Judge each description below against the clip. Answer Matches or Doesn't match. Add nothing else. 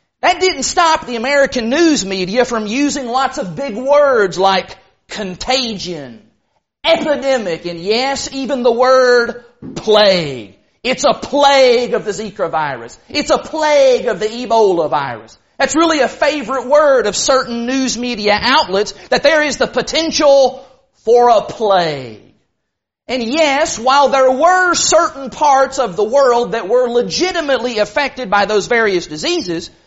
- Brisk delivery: Doesn't match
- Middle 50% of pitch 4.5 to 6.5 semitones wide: Matches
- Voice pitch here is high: Matches